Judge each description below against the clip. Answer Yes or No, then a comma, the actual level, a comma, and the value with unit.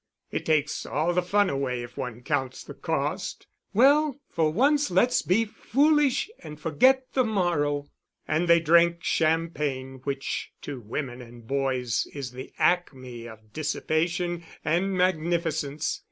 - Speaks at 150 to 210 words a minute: No, average, 140 wpm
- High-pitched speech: No, medium, 155 Hz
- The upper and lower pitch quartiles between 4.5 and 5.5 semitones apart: Yes, average, 5.1 semitones